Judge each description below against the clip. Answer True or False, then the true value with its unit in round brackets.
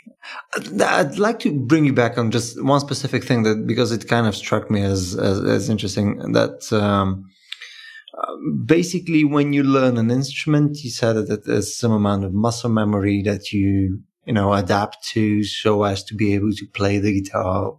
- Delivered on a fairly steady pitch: False (5.0 semitones)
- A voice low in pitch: True (110 Hz)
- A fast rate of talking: True (180 wpm)